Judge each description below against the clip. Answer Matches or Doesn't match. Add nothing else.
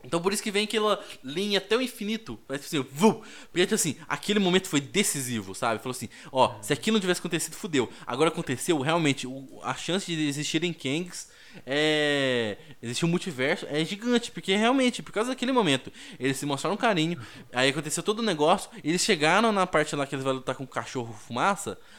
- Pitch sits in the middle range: Matches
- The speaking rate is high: Matches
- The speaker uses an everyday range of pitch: Doesn't match